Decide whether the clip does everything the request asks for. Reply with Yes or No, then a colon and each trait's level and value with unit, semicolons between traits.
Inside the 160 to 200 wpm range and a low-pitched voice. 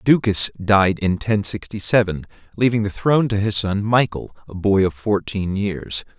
Yes: average, 175 wpm; low, 100 Hz